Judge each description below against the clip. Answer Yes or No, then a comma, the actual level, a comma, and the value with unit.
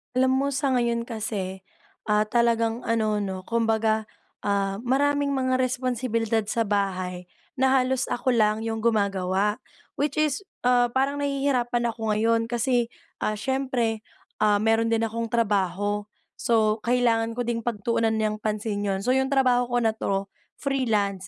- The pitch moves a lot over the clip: No, average, 2.9 semitones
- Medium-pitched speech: No, high, 230 Hz